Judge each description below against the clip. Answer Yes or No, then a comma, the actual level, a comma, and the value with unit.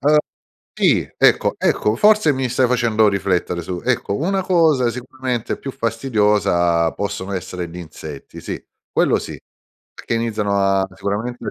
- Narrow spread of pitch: No, average, 5.3 semitones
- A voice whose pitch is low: Yes, low, 110 Hz